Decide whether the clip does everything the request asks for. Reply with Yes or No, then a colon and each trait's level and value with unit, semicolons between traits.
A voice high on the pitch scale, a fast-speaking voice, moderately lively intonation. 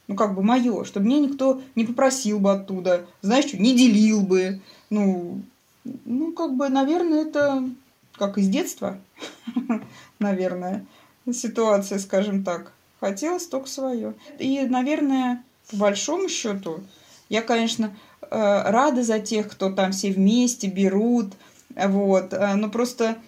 No: high, 225 Hz; average, 130 wpm; average, 4.7 semitones